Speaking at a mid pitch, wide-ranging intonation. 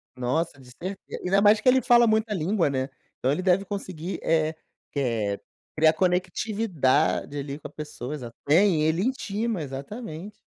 Yes: medium, 170 Hz; wide, 6.3 semitones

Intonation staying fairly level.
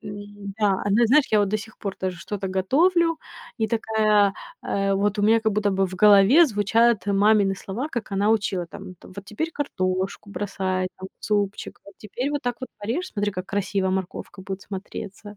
Yes: narrow, 2.2 semitones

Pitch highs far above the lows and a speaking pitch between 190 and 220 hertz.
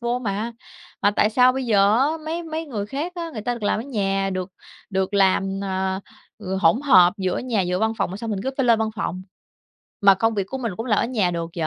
No: average, 4.2 semitones; high, 210 Hz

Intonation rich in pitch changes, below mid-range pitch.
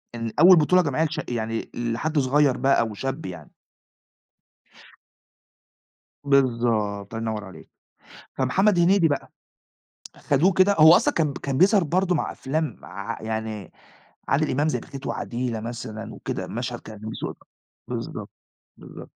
Yes: wide, 5.9 semitones; low, 130 Hz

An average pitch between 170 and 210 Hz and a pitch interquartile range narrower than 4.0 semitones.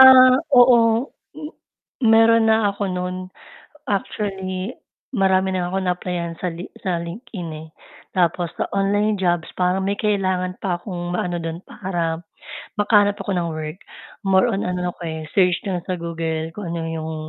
Yes: medium, 185 Hz; average, 2.9 semitones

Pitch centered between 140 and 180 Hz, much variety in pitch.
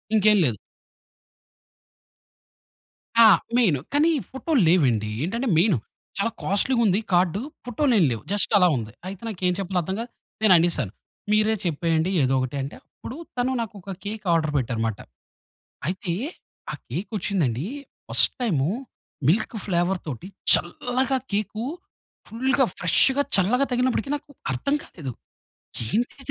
No: high, 190 Hz; wide, 6.1 semitones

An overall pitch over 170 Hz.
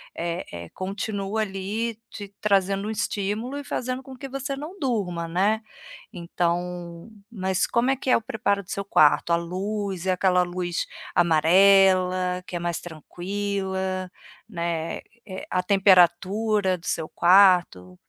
Yes: high, 190 Hz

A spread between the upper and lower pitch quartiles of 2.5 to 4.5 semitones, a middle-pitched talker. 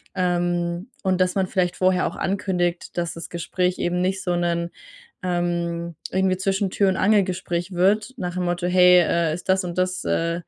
No: narrow, 1.3 semitones; medium, 180 Hz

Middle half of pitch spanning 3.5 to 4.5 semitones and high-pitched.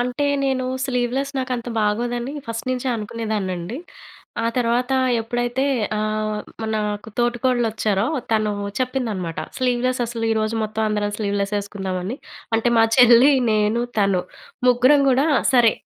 No: average, 2.8 semitones; high, 230 Hz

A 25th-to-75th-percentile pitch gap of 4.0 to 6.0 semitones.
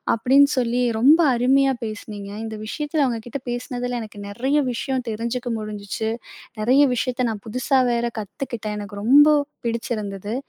No: average, 3.5 semitones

